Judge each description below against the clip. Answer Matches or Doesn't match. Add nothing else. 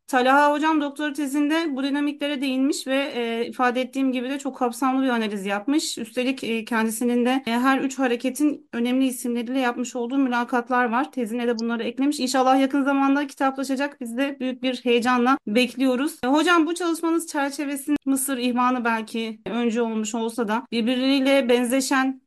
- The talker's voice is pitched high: Matches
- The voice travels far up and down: Doesn't match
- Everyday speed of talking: Doesn't match